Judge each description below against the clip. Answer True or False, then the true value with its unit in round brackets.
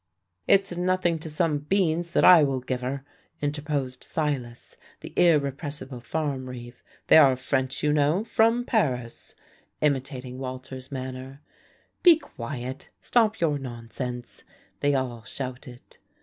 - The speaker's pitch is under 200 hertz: True (140 Hz)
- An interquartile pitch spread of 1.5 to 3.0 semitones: False (3.8 semitones)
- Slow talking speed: True (125 wpm)